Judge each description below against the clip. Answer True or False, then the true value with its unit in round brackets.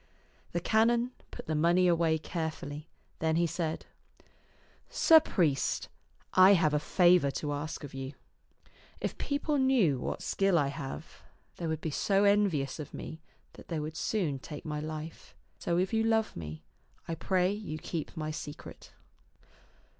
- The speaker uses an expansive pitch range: False (4.3 semitones)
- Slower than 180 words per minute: True (160 wpm)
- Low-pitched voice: False (165 Hz)